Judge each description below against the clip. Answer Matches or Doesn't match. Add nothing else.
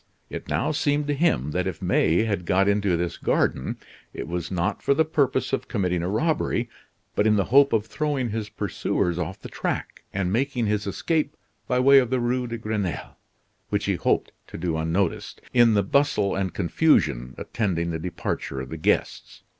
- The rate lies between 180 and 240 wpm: Matches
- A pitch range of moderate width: Doesn't match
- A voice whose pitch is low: Matches